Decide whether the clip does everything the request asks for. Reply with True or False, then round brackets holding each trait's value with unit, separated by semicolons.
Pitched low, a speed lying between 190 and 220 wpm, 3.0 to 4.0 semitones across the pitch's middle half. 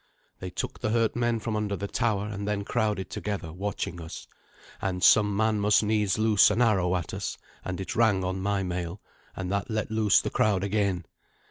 False (100 Hz; 200 wpm; 2.4 semitones)